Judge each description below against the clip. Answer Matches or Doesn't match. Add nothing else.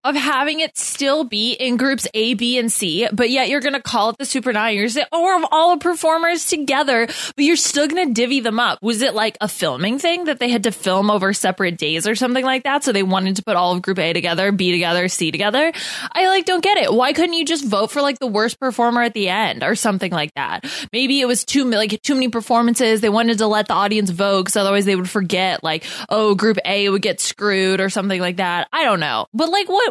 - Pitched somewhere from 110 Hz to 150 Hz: Doesn't match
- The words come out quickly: Matches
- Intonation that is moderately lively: Doesn't match